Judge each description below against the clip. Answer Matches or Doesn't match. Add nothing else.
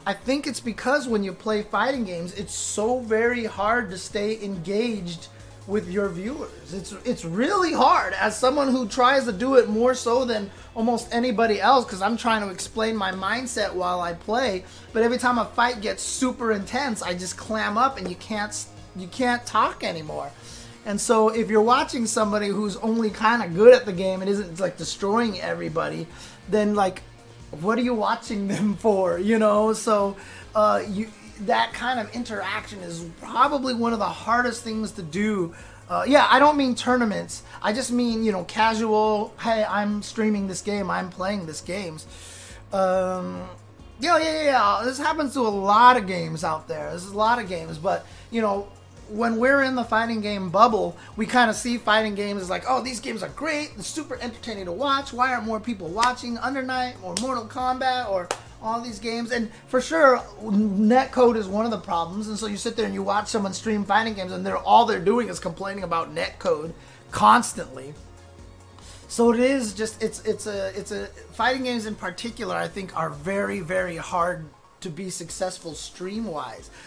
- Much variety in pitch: Doesn't match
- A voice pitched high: Matches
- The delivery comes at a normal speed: Matches